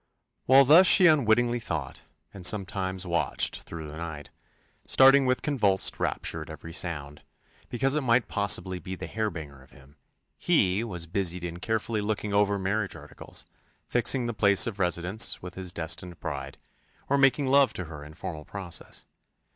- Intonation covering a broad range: Yes, wide, 5.7 semitones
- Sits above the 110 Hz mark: No, very low, 95 Hz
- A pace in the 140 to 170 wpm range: Yes, average, 165 wpm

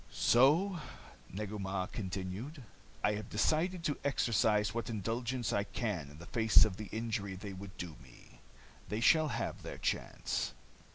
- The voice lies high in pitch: No, low, 105 Hz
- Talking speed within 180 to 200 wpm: No, average, 155 wpm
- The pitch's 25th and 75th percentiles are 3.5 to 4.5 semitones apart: Yes, average, 4.1 semitones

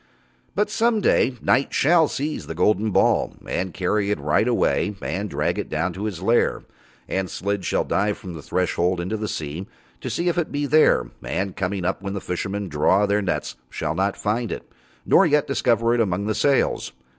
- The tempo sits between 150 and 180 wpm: No, average, 200 wpm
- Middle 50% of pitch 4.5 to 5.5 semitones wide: Yes, average, 5.1 semitones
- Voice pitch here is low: Yes, low, 100 Hz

